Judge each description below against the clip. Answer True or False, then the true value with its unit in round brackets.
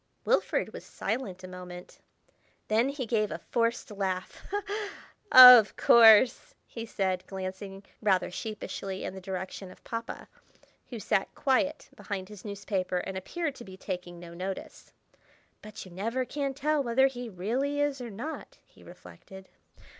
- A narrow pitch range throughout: False (4.8 semitones)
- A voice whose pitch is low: False (210 Hz)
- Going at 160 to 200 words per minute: False (145 wpm)